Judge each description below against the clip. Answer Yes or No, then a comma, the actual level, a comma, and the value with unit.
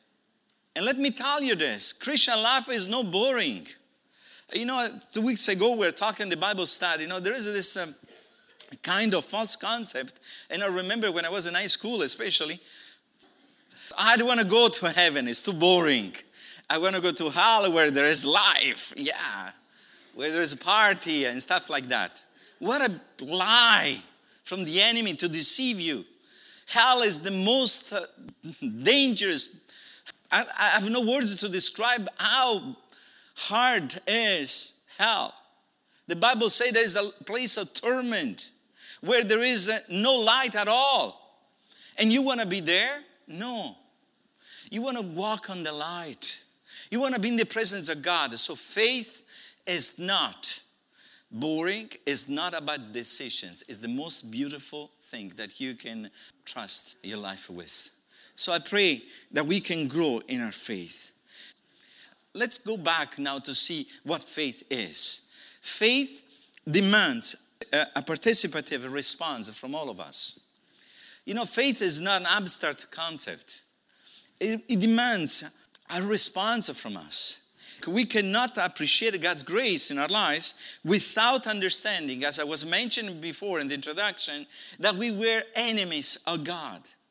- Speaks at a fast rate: No, average, 155 wpm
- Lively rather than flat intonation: Yes, wide, 6.0 semitones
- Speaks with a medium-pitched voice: No, high, 205 Hz